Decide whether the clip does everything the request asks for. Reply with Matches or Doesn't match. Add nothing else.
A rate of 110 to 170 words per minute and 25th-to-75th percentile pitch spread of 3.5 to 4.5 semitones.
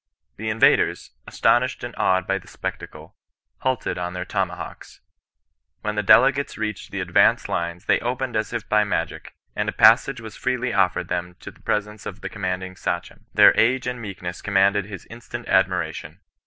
Doesn't match